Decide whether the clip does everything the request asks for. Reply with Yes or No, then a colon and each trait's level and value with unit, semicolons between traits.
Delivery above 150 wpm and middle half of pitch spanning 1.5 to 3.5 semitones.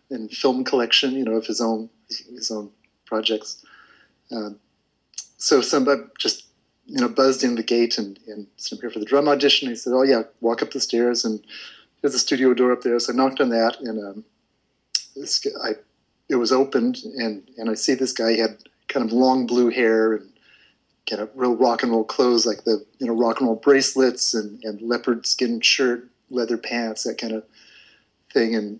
Yes: fast, 205 wpm; narrow, 2.4 semitones